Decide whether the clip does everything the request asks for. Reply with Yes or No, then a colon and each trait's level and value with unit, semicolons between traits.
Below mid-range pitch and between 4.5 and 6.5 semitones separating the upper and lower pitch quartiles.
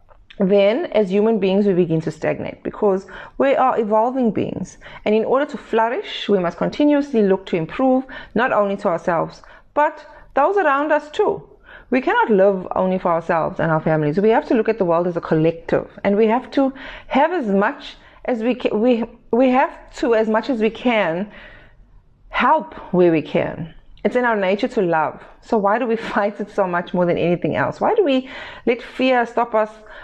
No: high, 220 Hz; average, 5.2 semitones